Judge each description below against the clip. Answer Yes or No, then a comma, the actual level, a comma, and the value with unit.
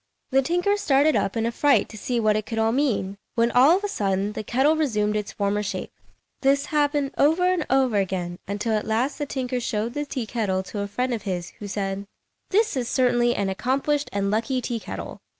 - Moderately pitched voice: No, high, 235 Hz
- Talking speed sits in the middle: No, fast, 220 wpm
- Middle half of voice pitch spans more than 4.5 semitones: Yes, average, 5.2 semitones